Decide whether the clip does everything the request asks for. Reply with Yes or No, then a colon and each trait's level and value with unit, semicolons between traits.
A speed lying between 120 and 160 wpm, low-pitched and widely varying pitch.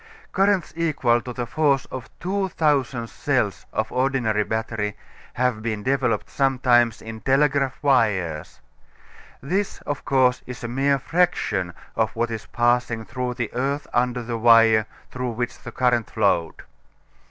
No: average, 140 wpm; low, 125 Hz; average, 3.2 semitones